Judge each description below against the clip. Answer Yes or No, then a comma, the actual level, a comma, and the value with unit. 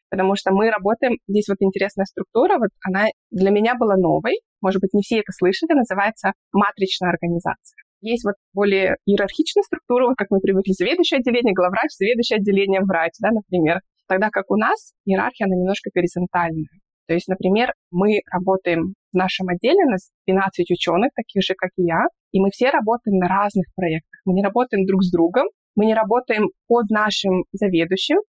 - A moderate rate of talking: No, fast, 180 wpm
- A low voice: No, high, 195 Hz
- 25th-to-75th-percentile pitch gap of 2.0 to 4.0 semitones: Yes, average, 3.3 semitones